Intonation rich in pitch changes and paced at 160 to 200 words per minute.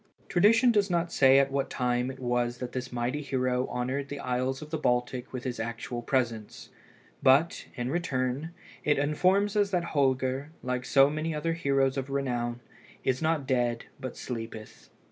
No: average, 3.4 semitones; average, 170 wpm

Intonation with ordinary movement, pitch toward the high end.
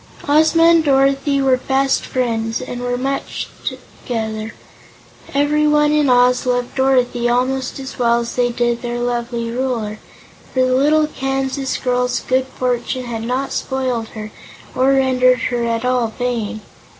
No: narrow, 2.1 semitones; very high, 255 Hz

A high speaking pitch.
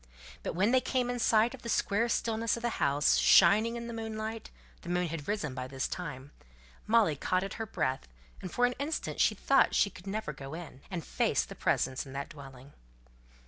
Yes: high, 195 Hz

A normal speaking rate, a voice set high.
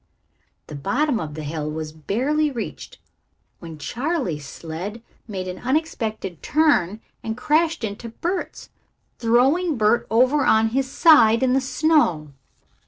No: slow, 130 wpm; high, 230 Hz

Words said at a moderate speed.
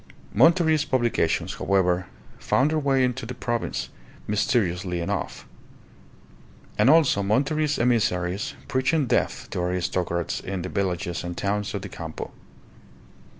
No: slow, 120 wpm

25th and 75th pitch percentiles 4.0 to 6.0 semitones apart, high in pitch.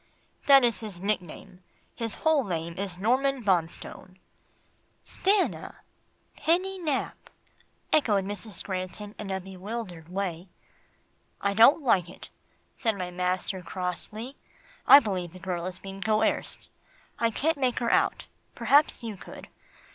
Yes: average, 4.9 semitones; high, 200 Hz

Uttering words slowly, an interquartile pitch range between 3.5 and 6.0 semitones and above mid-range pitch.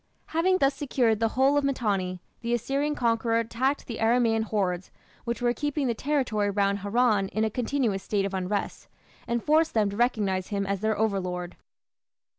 No: average, 175 wpm; average, 4.1 semitones; high, 225 Hz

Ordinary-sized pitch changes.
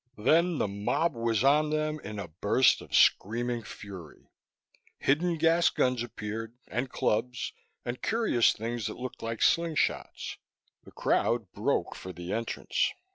No: wide, 6.2 semitones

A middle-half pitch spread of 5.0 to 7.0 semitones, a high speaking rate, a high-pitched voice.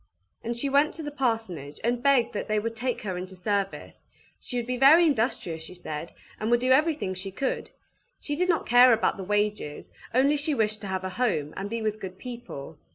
Yes: wide, 5.4 semitones; fast, 220 wpm; high, 225 Hz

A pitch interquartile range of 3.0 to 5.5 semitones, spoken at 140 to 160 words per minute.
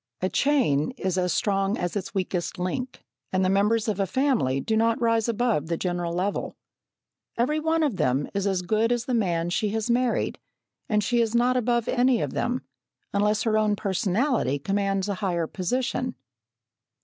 No: average, 4.5 semitones; average, 180 wpm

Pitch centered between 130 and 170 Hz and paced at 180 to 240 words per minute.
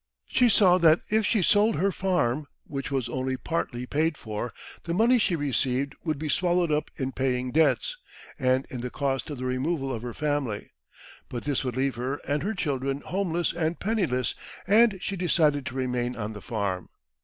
Yes: medium, 140 Hz; average, 190 wpm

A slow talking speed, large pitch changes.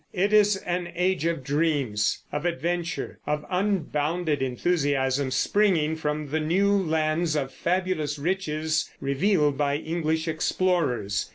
No: slow, 120 wpm; average, 3.4 semitones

